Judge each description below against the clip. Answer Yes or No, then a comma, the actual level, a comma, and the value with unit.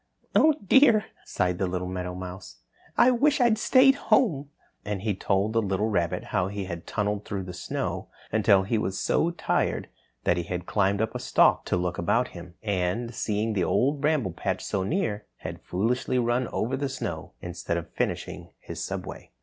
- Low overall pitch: Yes, low, 105 Hz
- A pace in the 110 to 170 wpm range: No, average, 180 wpm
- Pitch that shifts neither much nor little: No, wide, 5.8 semitones